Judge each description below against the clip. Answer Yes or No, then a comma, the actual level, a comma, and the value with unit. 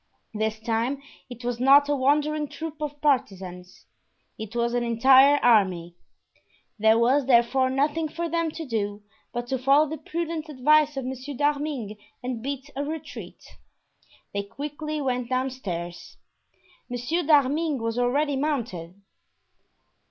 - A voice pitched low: No, very high, 265 Hz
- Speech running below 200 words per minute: Yes, slow, 135 wpm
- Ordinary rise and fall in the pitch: Yes, average, 4.2 semitones